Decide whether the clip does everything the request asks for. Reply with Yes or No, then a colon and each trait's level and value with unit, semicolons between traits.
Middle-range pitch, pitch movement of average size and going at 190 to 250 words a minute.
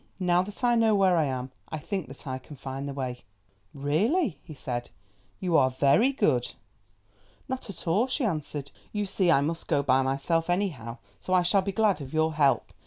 No: medium, 160 Hz; wide, 6.3 semitones; average, 195 wpm